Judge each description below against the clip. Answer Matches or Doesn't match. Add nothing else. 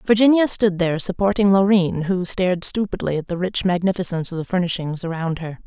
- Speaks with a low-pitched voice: Doesn't match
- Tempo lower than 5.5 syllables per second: Doesn't match